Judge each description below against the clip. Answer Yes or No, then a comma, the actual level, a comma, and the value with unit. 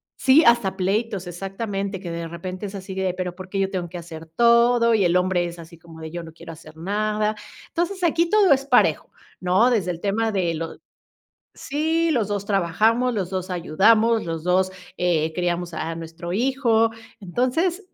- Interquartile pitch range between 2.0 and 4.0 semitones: No, average, 5.0 semitones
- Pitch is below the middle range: No, high, 190 Hz